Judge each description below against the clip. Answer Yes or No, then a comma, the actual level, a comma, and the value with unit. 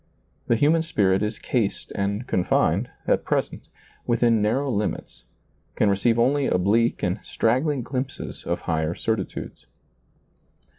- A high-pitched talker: No, low, 110 Hz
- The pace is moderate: No, slow, 120 wpm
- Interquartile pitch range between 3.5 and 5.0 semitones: Yes, average, 4.3 semitones